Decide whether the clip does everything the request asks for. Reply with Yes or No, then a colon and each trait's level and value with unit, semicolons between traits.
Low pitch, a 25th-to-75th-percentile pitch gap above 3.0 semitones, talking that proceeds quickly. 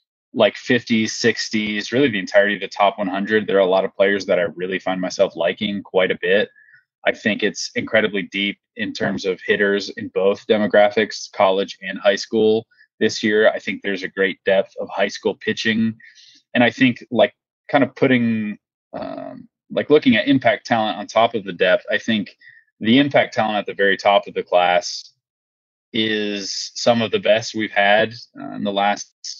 No: low, 110 Hz; average, 3.8 semitones; average, 190 wpm